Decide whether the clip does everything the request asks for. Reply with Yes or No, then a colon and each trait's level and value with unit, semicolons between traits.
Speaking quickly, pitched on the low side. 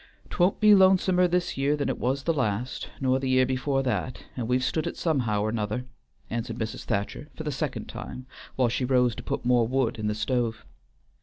Yes: fast, 210 wpm; low, 130 Hz